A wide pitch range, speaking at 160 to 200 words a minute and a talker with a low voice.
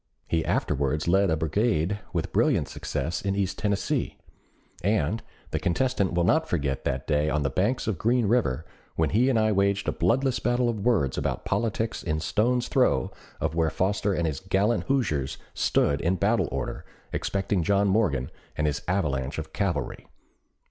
Yes: wide, 5.9 semitones; average, 170 wpm; very low, 95 Hz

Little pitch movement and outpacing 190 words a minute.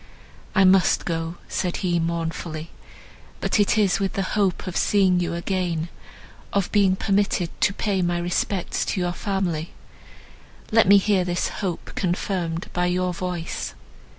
No: narrow, 2.2 semitones; average, 150 wpm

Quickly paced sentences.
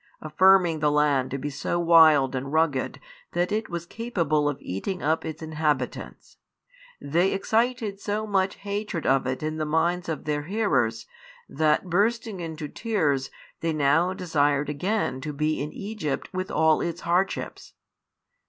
No: average, 155 wpm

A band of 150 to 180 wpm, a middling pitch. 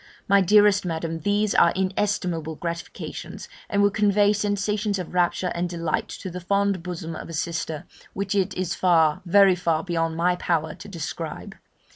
Yes: average, 170 wpm; medium, 180 Hz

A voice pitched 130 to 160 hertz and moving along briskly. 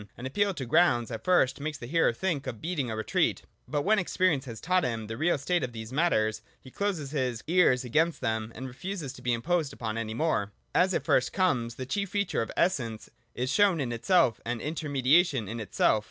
Yes: low, 135 Hz; fast, 215 wpm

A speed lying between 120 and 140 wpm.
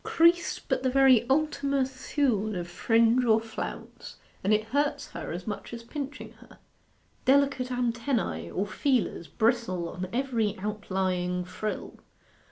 Yes: slow, 135 wpm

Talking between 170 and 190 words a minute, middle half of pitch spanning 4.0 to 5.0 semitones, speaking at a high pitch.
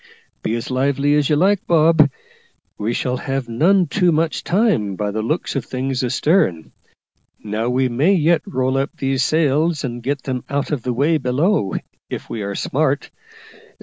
No: average, 175 wpm; average, 4.4 semitones; low, 135 Hz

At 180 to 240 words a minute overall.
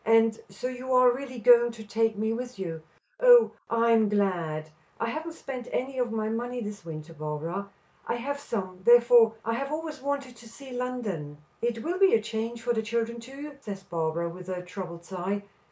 Yes: average, 200 wpm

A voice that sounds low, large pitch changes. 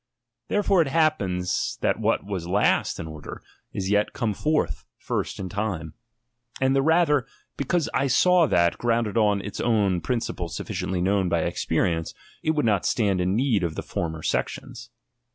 Yes: low, 105 Hz; wide, 7.0 semitones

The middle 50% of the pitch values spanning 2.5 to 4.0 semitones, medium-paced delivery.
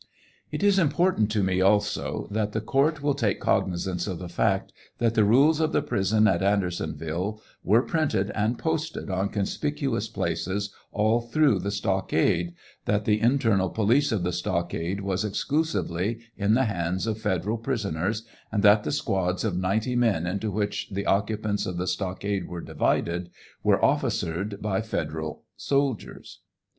Yes: average, 3.6 semitones; average, 155 wpm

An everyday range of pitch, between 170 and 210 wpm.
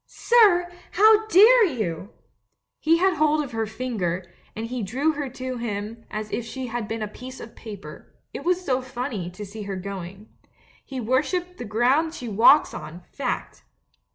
No: wide, 6.4 semitones; average, 180 wpm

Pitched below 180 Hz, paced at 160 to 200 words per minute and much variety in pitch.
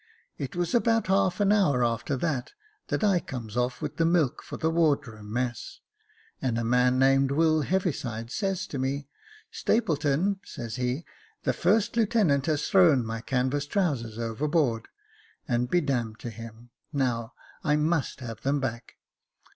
Yes: medium, 140 Hz; average, 165 wpm; wide, 6.0 semitones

